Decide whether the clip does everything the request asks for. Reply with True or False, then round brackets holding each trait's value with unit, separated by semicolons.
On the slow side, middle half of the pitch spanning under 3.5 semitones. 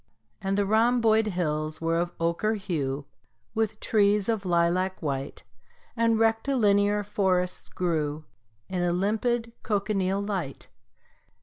False (115 wpm; 4.0 semitones)